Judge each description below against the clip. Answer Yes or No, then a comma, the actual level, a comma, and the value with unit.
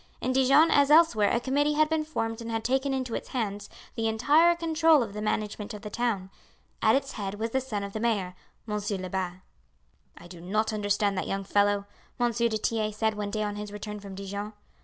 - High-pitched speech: Yes, high, 220 Hz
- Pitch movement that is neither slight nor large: Yes, average, 4.2 semitones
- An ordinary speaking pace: No, fast, 215 wpm